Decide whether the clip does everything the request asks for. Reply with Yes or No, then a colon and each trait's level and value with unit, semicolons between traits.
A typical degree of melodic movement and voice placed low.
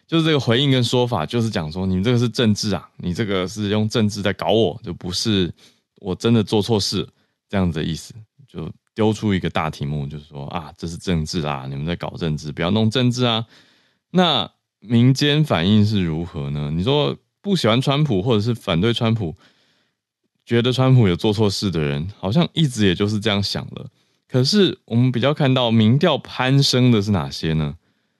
No: wide, 5.9 semitones; low, 110 Hz